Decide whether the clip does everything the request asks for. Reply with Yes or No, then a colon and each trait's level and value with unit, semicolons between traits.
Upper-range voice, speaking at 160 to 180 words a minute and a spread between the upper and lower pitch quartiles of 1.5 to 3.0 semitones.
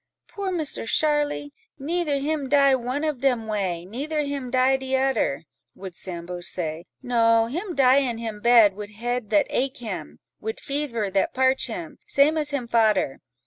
No: very high, 250 Hz; average, 170 wpm; average, 5.0 semitones